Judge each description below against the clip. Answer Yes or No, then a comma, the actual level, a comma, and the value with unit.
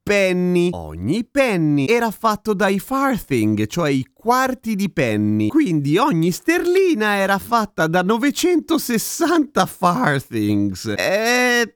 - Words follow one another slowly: Yes, slow, 105 wpm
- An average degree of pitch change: No, wide, 8.0 semitones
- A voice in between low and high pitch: No, high, 200 Hz